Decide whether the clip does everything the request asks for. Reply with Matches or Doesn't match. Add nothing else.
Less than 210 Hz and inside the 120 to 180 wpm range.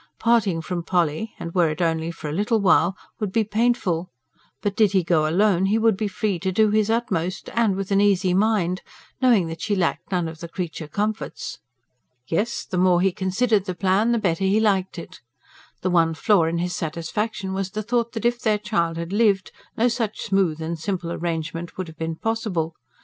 Doesn't match